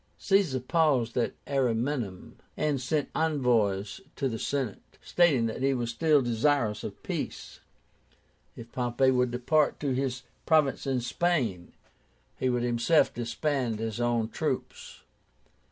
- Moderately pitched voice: No, low, 125 Hz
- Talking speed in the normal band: No, slow, 130 wpm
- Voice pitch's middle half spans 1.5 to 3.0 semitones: No, average, 3.7 semitones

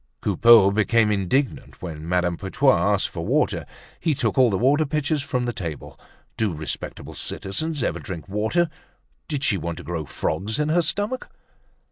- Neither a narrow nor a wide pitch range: No, wide, 8.1 semitones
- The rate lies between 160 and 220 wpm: Yes, average, 165 wpm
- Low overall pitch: Yes, low, 110 Hz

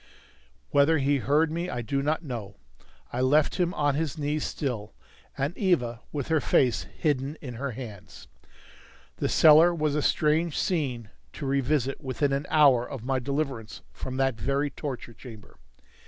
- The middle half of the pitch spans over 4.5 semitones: No, average, 3.4 semitones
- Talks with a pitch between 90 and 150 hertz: Yes, medium, 140 Hz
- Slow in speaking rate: No, average, 160 wpm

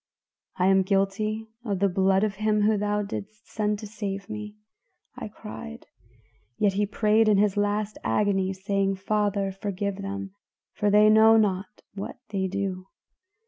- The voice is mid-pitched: No, high, 205 Hz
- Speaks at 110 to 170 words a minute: Yes, average, 155 wpm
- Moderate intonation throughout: No, narrow, 1.5 semitones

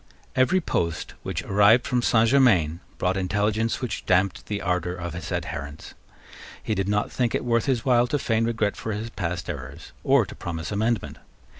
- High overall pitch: No, low, 105 Hz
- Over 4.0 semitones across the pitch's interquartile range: Yes, average, 4.8 semitones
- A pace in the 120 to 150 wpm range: No, average, 180 wpm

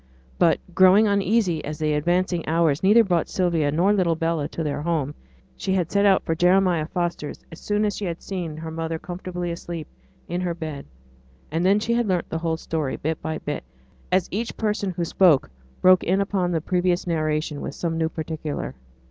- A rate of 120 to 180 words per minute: No, average, 195 wpm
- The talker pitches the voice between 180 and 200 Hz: No, medium, 170 Hz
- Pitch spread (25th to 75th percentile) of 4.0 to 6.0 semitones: No, average, 2.8 semitones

